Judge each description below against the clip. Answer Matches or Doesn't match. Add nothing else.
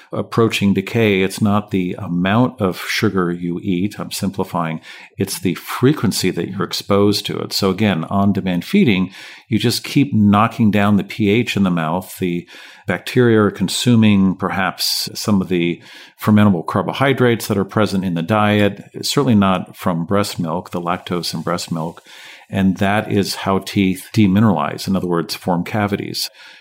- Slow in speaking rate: Doesn't match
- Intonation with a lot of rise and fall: Doesn't match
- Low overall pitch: Matches